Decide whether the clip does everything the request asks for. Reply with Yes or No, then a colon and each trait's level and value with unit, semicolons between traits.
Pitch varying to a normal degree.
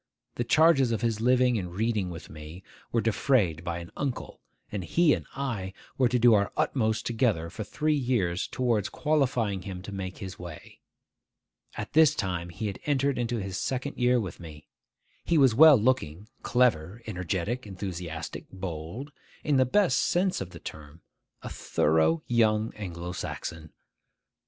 No: wide, 6.2 semitones